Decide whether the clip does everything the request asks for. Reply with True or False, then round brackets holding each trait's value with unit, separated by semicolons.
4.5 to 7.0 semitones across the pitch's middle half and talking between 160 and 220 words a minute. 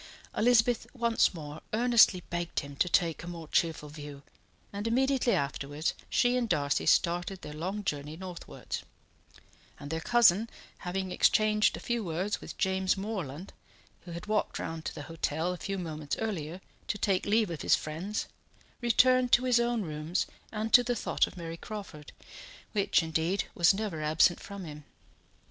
True (5.2 semitones; 165 wpm)